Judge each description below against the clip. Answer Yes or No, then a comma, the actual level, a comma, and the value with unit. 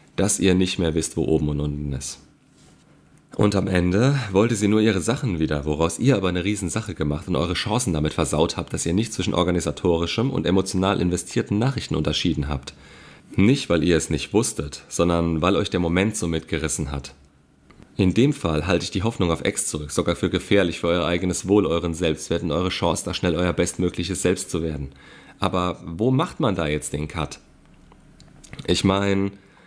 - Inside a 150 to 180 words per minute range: No, fast, 190 wpm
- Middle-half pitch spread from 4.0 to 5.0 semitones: No, average, 3.3 semitones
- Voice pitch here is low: Yes, very low, 90 Hz